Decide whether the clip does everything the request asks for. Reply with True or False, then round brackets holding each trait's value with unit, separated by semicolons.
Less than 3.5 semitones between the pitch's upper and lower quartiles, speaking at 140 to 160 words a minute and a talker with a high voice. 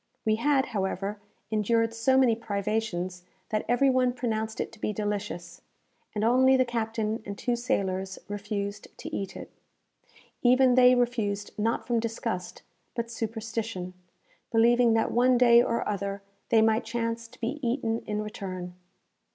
True (2.7 semitones; 150 wpm; 225 Hz)